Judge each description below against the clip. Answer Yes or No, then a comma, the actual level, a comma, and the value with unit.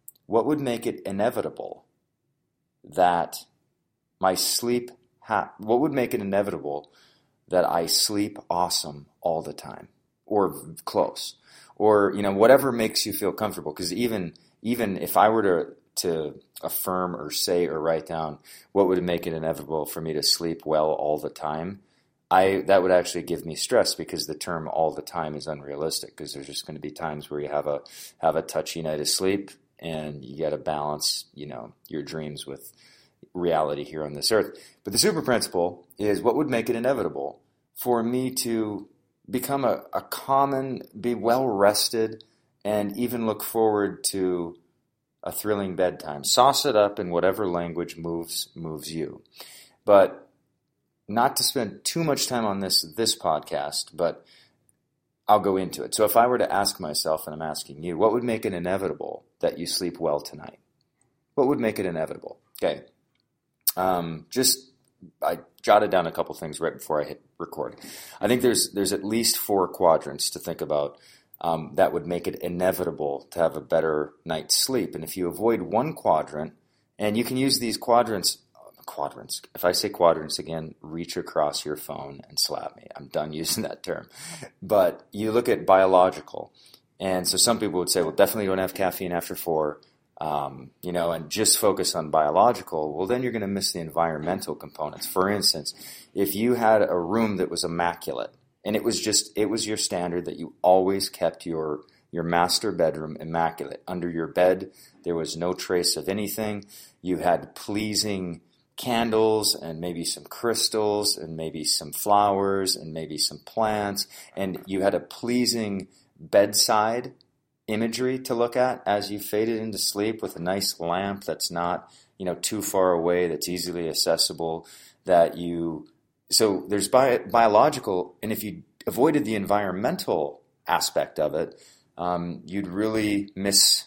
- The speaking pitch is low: Yes, very low, 95 Hz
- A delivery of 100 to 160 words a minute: No, average, 175 wpm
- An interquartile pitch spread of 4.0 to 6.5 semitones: Yes, average, 4.9 semitones